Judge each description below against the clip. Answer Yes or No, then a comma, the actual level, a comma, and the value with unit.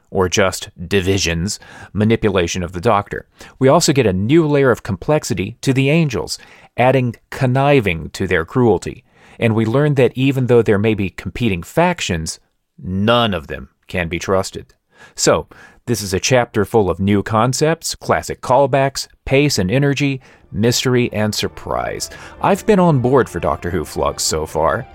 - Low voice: Yes, low, 115 Hz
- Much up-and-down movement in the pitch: Yes, wide, 5.9 semitones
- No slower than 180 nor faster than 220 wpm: No, average, 160 wpm